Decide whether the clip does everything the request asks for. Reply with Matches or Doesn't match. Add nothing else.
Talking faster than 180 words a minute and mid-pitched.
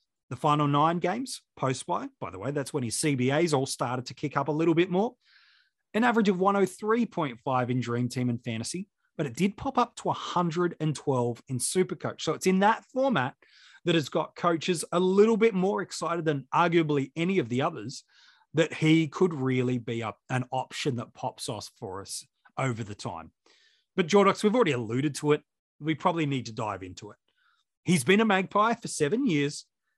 Matches